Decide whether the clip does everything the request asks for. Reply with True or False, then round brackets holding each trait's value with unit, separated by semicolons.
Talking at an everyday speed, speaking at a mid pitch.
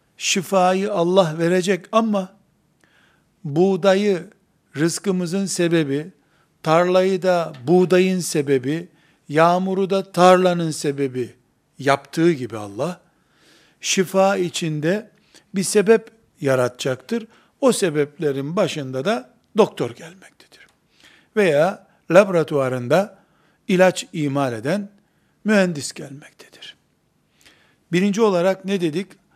False (80 wpm; 175 Hz)